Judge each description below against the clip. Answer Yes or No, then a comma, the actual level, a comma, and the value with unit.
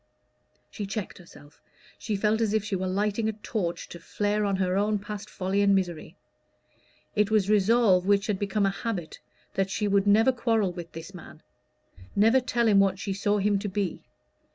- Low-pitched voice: No, high, 200 Hz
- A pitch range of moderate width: No, narrow, 2.0 semitones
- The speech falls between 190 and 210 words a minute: Yes, average, 195 wpm